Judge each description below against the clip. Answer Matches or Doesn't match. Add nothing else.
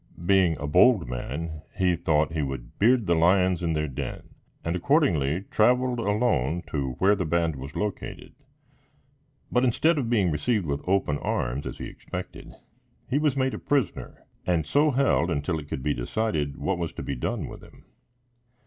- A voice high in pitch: Doesn't match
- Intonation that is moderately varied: Doesn't match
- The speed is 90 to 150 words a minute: Doesn't match